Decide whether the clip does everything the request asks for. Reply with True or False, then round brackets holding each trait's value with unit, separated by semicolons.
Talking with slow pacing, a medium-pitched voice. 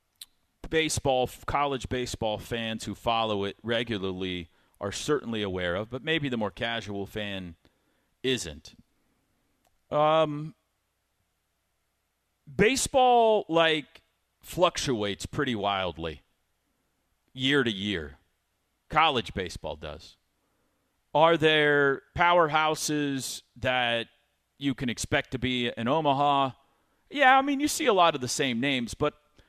False (110 wpm; 120 Hz)